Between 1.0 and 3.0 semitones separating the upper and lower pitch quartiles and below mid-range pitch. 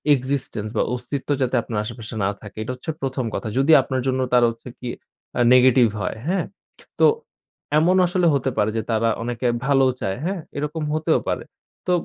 No: average, 3.4 semitones; low, 130 Hz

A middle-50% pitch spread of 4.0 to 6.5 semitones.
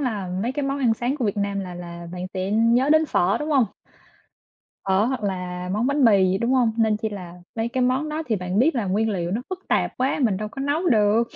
Yes: average, 5.2 semitones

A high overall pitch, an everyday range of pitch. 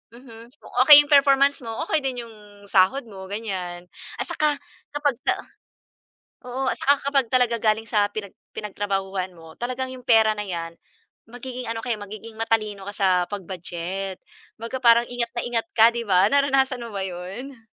Yes: high, 225 Hz; average, 4.2 semitones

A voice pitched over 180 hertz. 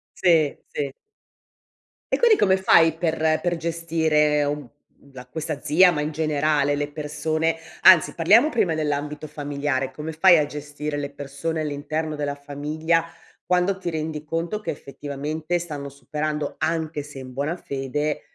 No: medium, 150 Hz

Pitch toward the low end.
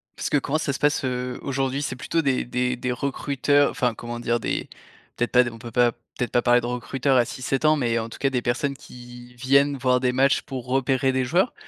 Yes: low, 125 Hz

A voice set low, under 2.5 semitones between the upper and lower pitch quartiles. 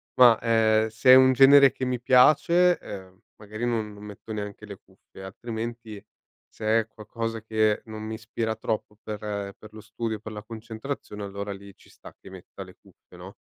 Yes: low, 110 Hz; narrow, 2.0 semitones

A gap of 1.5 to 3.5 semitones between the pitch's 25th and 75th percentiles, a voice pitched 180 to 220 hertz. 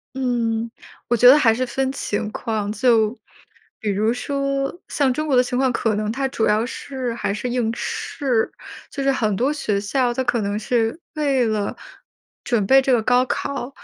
No: average, 3.2 semitones; high, 245 Hz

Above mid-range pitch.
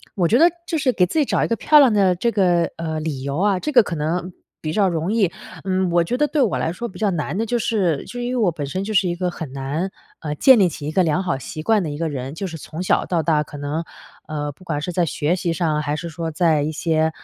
No: medium, 170 Hz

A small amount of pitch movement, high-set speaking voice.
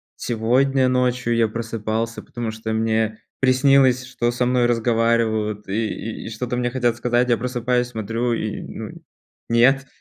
No: narrow, 2.0 semitones; low, 120 Hz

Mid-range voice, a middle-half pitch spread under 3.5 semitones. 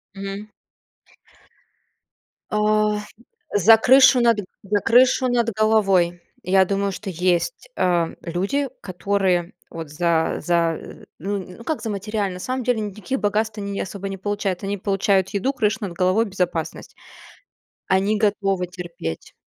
No: high, 200 Hz; average, 3.0 semitones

